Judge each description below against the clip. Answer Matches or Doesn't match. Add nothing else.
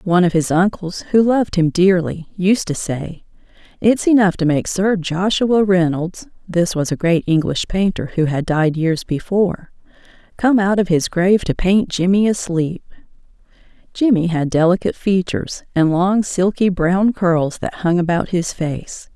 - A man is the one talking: Doesn't match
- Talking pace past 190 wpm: Doesn't match